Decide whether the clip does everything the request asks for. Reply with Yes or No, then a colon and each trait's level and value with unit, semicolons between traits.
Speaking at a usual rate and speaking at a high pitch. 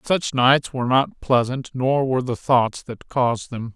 No: average, 190 wpm; low, 125 Hz